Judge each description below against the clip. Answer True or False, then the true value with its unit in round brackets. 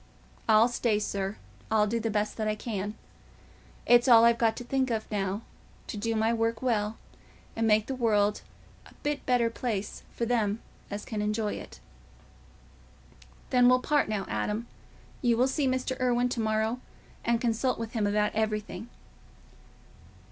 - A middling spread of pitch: False (2.3 semitones)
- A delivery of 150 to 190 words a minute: True (155 wpm)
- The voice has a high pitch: True (225 Hz)